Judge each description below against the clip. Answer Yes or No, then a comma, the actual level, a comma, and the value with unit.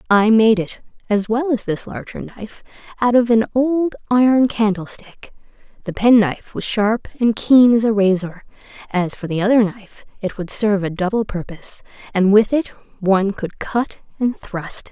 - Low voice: No, high, 215 Hz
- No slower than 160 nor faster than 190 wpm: Yes, average, 175 wpm